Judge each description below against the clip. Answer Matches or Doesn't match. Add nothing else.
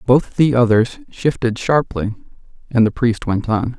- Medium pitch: Doesn't match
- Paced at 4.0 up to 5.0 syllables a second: Matches